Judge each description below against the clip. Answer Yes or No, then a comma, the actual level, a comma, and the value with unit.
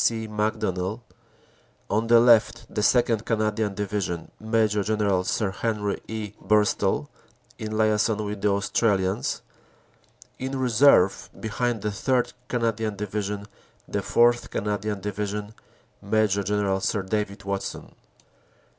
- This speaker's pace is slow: Yes, slow, 115 wpm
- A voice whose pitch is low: Yes, low, 105 Hz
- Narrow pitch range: Yes, narrow, 1.7 semitones